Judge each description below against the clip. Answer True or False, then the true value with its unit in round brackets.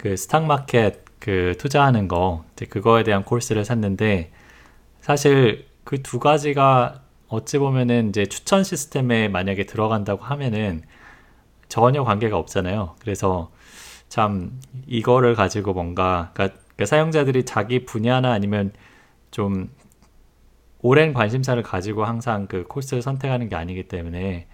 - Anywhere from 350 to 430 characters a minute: False (295 characters per minute)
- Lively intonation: False (4.9 semitones)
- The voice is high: False (110 Hz)